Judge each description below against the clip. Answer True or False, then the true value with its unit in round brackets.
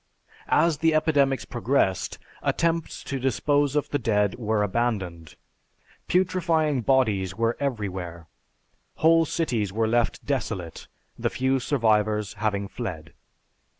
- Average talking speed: False (115 wpm)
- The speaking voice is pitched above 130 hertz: False (120 Hz)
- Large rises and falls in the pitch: True (5.7 semitones)